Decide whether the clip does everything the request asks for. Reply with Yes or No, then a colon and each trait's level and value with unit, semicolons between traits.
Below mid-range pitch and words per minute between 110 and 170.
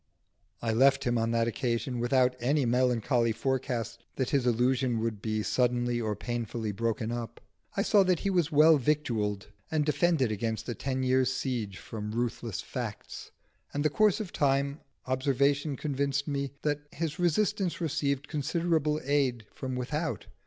Yes: low, 130 Hz; average, 160 wpm